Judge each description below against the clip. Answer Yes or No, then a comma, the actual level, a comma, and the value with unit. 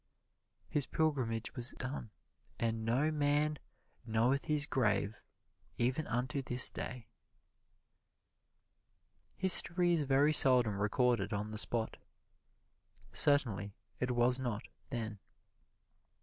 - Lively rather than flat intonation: No, average, 4.3 semitones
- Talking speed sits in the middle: No, slow, 100 wpm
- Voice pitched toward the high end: No, low, 125 Hz